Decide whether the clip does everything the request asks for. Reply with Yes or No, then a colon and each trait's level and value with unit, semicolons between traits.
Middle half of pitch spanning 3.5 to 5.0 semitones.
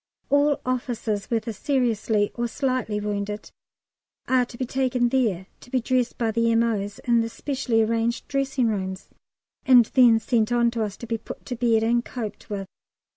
No: narrow, 2.5 semitones